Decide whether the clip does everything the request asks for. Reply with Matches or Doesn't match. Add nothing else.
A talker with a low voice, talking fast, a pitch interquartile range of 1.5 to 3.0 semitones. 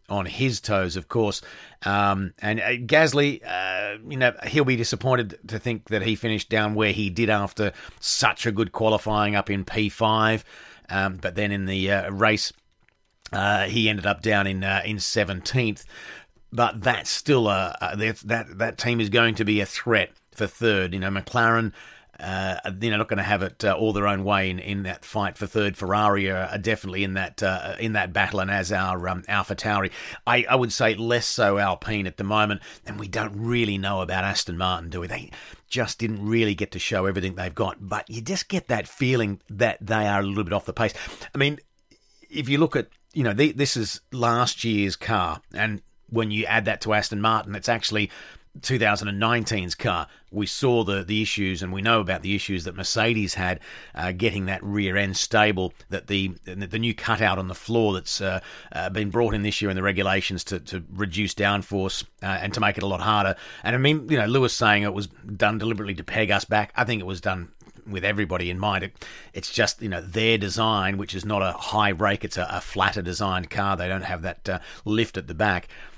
Matches